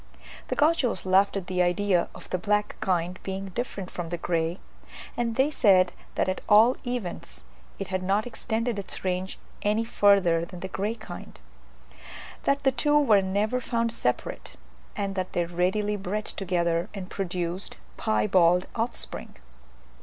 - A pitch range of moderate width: Yes, average, 3.6 semitones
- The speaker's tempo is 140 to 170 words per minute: Yes, average, 155 wpm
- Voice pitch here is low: No, high, 195 Hz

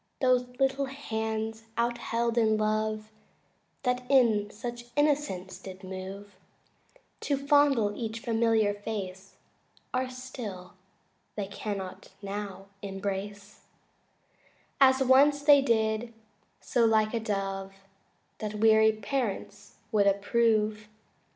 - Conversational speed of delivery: No, slow, 105 wpm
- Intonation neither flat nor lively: Yes, average, 3.4 semitones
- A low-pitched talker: No, high, 220 Hz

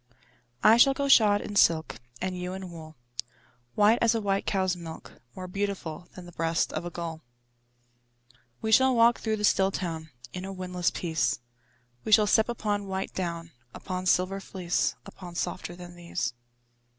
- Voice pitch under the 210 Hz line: Yes, medium, 185 Hz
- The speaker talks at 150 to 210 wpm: Yes, average, 170 wpm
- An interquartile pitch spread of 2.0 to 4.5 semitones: Yes, average, 3.1 semitones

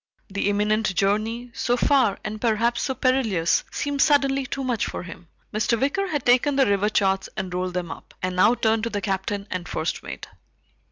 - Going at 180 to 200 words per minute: Yes, average, 190 wpm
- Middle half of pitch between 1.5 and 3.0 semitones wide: No, average, 4.9 semitones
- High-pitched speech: Yes, high, 215 Hz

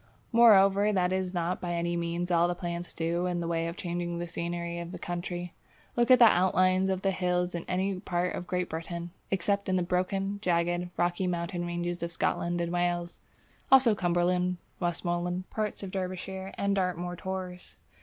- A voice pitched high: No, medium, 180 Hz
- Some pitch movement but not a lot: No, narrow, 1.5 semitones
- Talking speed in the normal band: Yes, average, 185 wpm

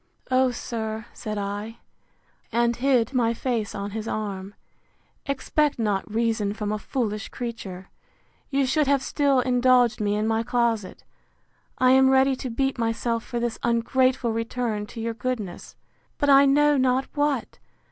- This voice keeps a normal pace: Yes, average, 150 wpm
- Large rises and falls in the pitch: No, average, 3.1 semitones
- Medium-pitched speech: No, high, 235 Hz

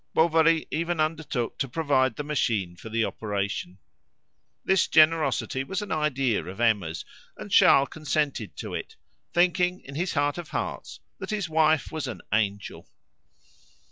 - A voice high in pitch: No, medium, 145 Hz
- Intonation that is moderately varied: No, wide, 6.3 semitones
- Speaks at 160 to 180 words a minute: No, average, 145 wpm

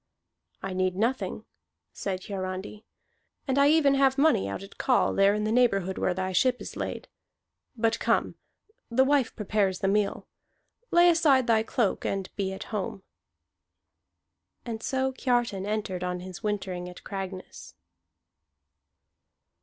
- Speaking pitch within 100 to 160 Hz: No, high, 210 Hz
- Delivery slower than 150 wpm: Yes, average, 140 wpm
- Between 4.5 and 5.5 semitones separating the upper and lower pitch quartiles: Yes, average, 5.1 semitones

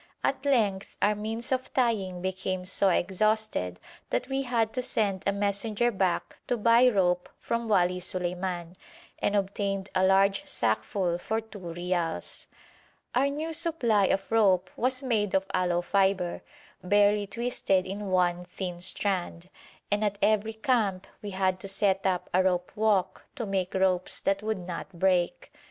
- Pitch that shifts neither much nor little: Yes, average, 3.0 semitones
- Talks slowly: No, average, 155 wpm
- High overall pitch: Yes, high, 195 Hz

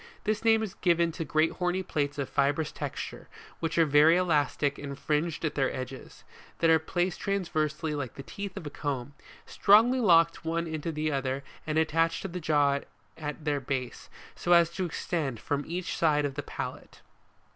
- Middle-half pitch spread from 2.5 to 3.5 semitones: Yes, average, 2.9 semitones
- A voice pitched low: No, medium, 160 Hz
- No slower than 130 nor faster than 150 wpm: No, average, 195 wpm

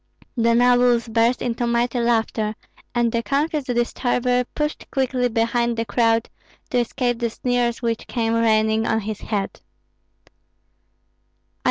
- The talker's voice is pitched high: Yes, high, 235 Hz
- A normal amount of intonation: No, narrow, 1.4 semitones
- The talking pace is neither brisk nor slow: No, slow, 130 wpm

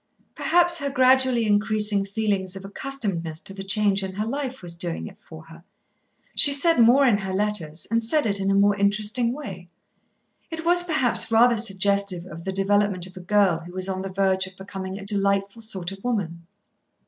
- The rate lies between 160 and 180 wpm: No, average, 195 wpm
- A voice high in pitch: Yes, high, 200 Hz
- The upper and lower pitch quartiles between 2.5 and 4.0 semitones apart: Yes, average, 3.6 semitones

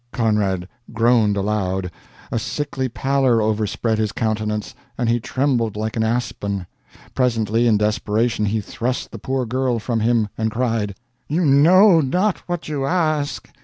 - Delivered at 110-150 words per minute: Yes, average, 145 wpm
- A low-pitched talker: Yes, low, 115 Hz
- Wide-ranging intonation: No, average, 3.7 semitones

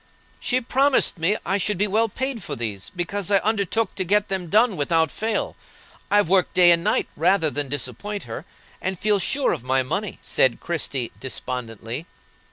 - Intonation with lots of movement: Yes, wide, 6.3 semitones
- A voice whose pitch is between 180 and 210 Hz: Yes, medium, 185 Hz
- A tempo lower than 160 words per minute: No, average, 175 wpm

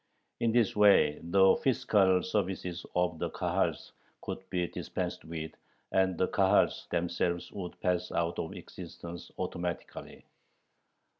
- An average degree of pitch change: No, narrow, 1.9 semitones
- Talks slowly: Yes, slow, 125 wpm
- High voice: No, very low, 90 Hz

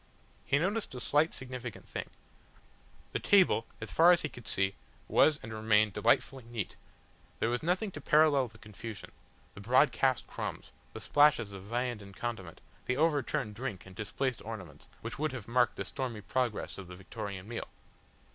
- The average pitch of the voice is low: Yes, low, 120 Hz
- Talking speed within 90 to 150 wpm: No, average, 170 wpm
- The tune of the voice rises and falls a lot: No, average, 5.0 semitones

